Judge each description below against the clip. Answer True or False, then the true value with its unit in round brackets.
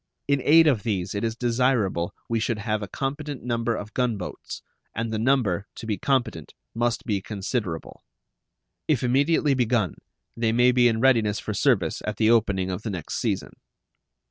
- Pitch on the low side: True (115 Hz)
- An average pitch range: True (3.4 semitones)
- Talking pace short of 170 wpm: False (175 wpm)